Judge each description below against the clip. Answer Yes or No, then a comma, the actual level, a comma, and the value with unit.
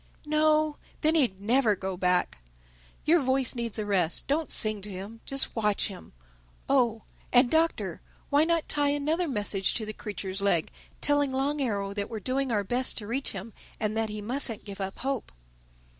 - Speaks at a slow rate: No, average, 175 wpm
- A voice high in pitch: Yes, high, 230 Hz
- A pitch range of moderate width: No, wide, 5.7 semitones